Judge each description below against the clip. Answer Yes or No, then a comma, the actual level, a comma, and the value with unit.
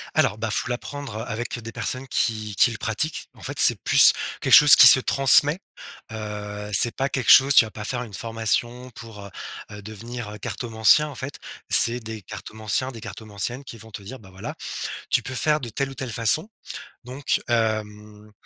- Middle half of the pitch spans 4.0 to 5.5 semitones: No, average, 3.2 semitones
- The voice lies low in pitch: Yes, low, 115 Hz